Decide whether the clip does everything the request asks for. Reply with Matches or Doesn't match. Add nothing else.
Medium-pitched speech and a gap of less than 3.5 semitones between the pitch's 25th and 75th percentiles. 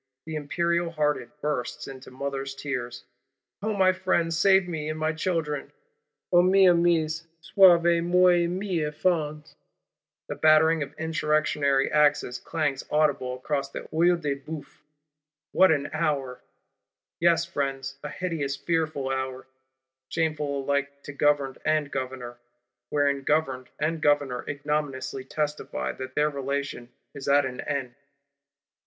Matches